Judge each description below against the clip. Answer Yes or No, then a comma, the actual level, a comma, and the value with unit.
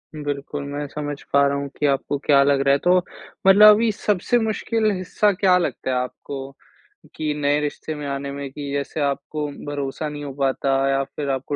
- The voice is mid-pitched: Yes, medium, 145 Hz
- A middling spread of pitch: No, narrow, 2.2 semitones